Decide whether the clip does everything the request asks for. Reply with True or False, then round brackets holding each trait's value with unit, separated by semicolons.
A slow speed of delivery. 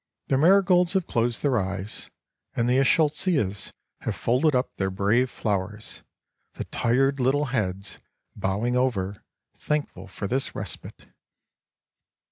True (120 wpm)